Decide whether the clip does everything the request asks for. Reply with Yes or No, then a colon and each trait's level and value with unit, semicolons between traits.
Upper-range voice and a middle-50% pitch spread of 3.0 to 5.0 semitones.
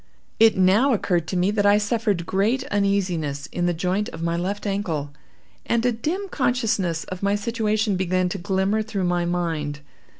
Yes: high, 195 Hz; average, 3.6 semitones